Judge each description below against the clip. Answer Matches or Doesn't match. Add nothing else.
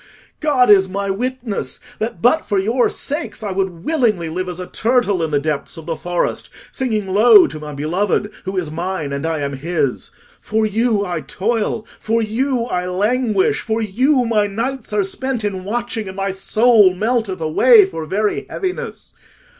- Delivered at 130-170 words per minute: Doesn't match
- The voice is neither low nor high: Doesn't match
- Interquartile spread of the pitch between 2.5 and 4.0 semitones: Doesn't match